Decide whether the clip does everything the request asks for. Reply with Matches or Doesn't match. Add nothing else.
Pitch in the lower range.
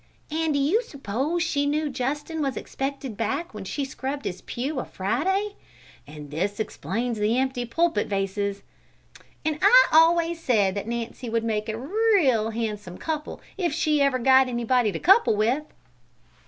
Doesn't match